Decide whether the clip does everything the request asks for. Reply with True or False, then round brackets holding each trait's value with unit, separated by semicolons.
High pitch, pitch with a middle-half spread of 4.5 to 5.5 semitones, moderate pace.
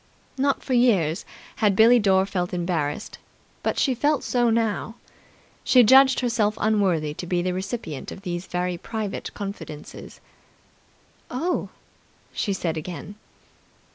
False (200 Hz; 5.1 semitones; 130 wpm)